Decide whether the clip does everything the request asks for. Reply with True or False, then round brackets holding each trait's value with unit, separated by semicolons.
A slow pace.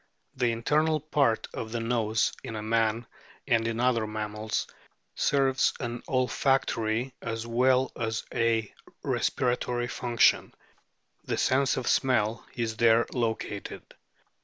True (115 wpm)